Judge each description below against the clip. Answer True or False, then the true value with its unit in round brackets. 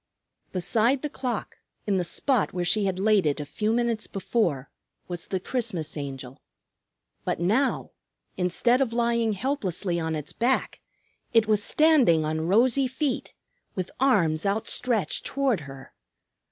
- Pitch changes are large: True (6.0 semitones)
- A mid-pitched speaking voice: False (210 Hz)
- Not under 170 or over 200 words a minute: False (140 wpm)